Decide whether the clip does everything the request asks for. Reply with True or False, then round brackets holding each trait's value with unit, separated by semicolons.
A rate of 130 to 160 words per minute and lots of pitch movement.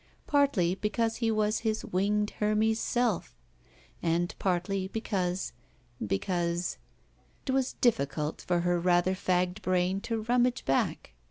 False (135 wpm; 4.0 semitones)